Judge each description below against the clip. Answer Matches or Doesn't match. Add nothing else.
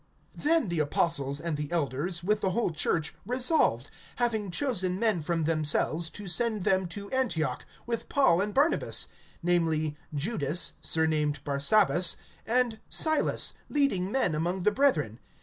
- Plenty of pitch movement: Matches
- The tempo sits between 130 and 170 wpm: Matches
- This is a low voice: Doesn't match